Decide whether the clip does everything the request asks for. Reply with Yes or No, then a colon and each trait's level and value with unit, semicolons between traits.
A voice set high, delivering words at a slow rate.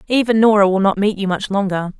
No: high, 200 Hz; fast, 240 wpm